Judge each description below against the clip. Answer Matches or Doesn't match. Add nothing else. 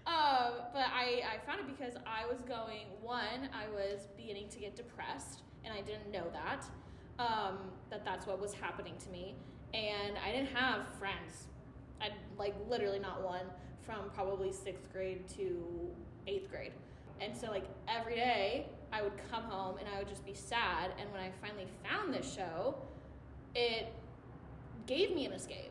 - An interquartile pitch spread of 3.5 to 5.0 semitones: Matches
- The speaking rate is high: Doesn't match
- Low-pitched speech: Doesn't match